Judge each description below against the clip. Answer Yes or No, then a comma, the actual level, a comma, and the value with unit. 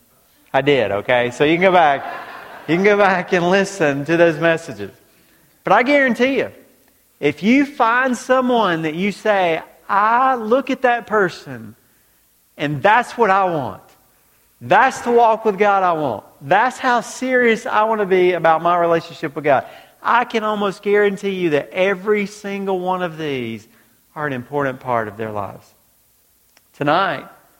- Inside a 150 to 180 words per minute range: Yes, average, 165 wpm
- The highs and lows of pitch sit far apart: Yes, wide, 6.9 semitones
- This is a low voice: No, medium, 185 Hz